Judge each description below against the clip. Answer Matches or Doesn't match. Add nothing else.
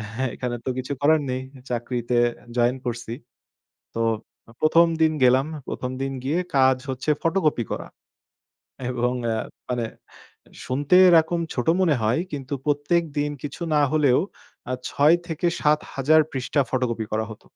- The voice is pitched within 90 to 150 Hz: Matches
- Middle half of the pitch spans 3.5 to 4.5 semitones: Matches